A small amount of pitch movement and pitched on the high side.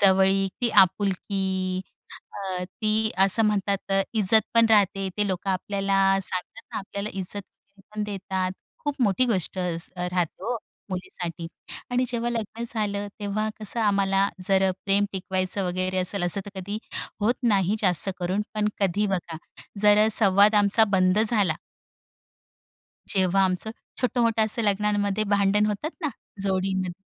Yes: narrow, 2.1 semitones; high, 200 Hz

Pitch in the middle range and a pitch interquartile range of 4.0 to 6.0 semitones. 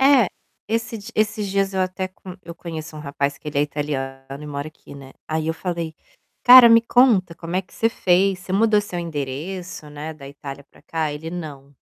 Yes: medium, 170 Hz; average, 4.9 semitones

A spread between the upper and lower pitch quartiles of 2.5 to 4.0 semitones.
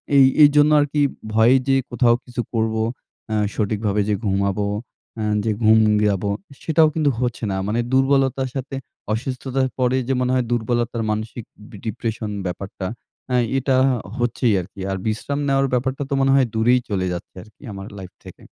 Yes: average, 3.7 semitones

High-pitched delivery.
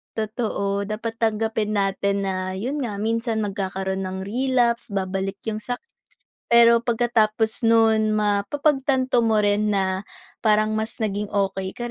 Yes: high, 215 Hz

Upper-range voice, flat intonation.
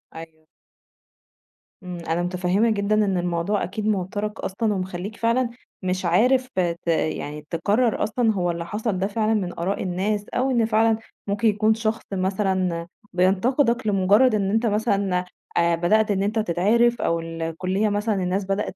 No: high, 200 Hz; average, 3.3 semitones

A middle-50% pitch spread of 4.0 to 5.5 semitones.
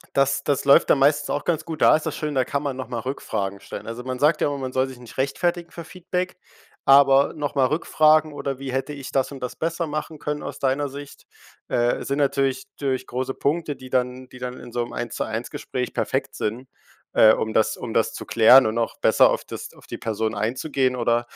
No: average, 2.7 semitones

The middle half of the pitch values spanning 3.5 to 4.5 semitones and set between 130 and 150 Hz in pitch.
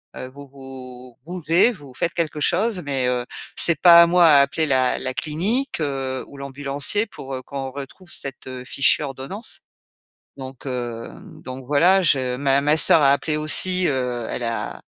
Yes: average, 4.1 semitones; medium, 140 Hz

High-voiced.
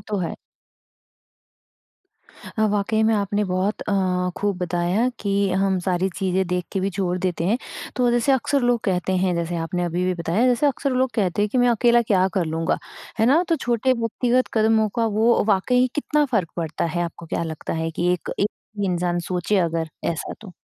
Yes: high, 200 Hz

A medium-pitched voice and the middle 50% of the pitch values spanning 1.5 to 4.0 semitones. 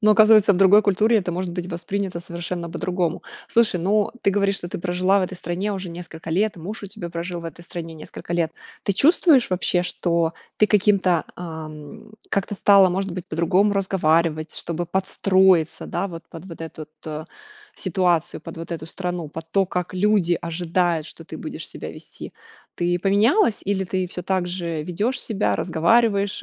Yes: medium, 180 Hz; average, 2.8 semitones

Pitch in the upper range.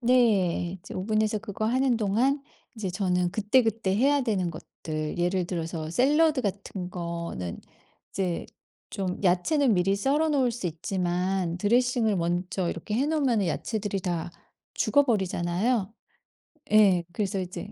Yes: high, 195 Hz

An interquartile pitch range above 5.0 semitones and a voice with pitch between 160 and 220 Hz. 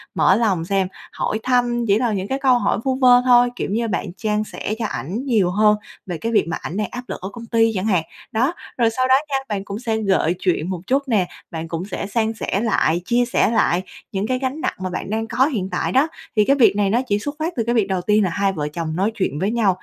No: average, 4.2 semitones; high, 215 Hz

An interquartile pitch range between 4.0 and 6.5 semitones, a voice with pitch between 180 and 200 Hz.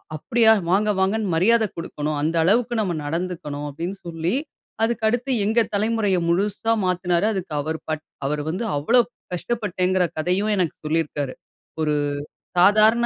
Yes: average, 5.0 semitones; medium, 185 Hz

